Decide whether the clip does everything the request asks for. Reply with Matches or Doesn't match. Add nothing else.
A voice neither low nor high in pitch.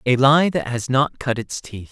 Doesn't match